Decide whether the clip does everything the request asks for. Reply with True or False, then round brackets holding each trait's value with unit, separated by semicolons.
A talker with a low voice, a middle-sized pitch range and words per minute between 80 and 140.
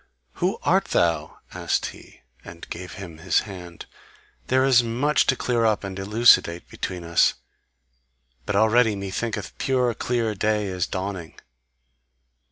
True (100 Hz; 4.4 semitones; 135 wpm)